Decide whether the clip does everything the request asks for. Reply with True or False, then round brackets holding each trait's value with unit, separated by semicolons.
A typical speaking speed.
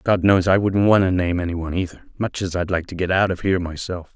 False (290 wpm)